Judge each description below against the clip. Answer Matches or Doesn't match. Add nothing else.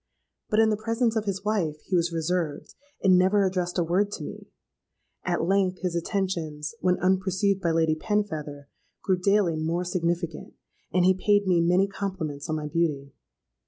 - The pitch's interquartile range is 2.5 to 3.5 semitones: Matches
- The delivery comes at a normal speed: Matches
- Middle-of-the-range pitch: Matches